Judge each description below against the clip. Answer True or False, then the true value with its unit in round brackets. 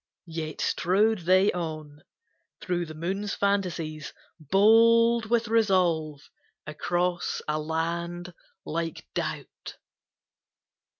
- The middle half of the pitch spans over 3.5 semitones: True (4.1 semitones)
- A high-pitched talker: False (175 Hz)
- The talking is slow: True (85 wpm)